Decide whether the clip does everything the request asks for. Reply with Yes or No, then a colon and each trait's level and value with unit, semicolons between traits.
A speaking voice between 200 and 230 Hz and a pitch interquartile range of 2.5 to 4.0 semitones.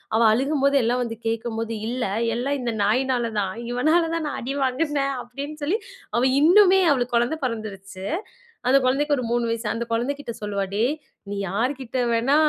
No: very high, 250 Hz; average, 3.7 semitones